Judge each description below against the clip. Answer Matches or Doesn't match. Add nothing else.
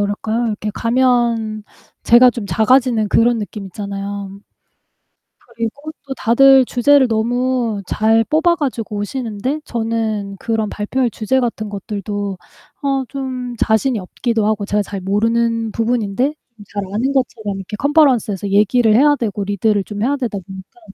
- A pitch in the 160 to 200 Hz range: Doesn't match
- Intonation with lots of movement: Doesn't match